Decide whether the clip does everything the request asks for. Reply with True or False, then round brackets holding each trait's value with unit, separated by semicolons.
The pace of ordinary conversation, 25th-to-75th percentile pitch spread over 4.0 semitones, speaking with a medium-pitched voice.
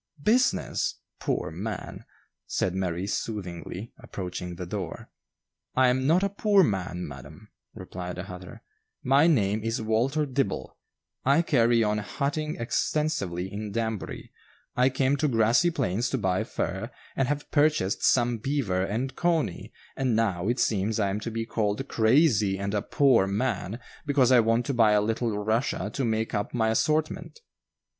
False (155 wpm; 5.4 semitones; 115 Hz)